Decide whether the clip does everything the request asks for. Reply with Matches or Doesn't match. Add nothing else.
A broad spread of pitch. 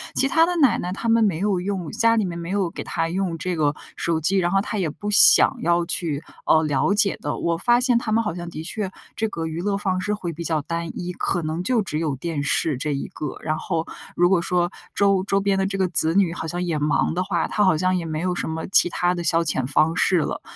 Doesn't match